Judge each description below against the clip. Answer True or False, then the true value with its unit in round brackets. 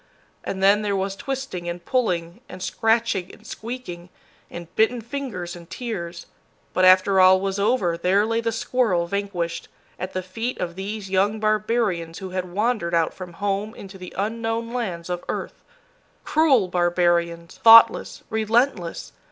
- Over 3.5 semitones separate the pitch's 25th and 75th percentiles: True (4.3 semitones)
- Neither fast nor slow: True (150 wpm)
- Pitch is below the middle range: False (195 Hz)